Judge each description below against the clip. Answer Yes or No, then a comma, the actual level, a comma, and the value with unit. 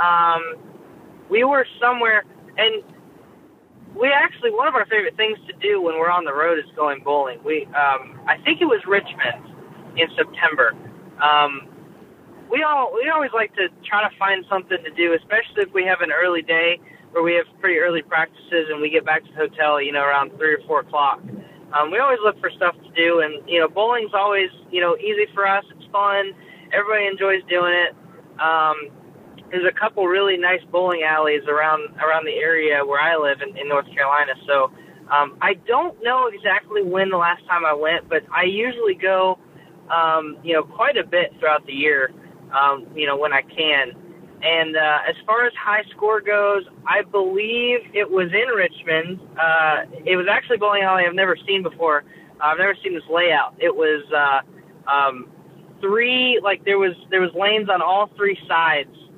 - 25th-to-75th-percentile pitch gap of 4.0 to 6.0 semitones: Yes, average, 4.5 semitones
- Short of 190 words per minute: No, average, 195 wpm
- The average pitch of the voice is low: No, medium, 180 Hz